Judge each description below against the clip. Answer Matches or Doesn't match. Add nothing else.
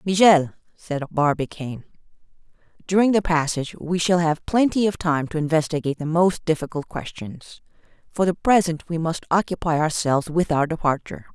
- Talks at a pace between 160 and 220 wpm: Doesn't match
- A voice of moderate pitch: Matches